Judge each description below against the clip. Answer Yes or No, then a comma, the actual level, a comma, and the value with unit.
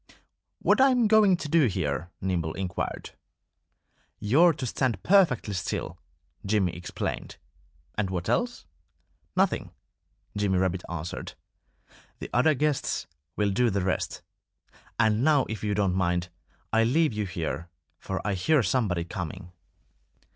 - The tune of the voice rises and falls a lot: Yes, wide, 7.4 semitones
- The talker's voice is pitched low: Yes, low, 105 Hz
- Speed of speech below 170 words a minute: Yes, slow, 135 wpm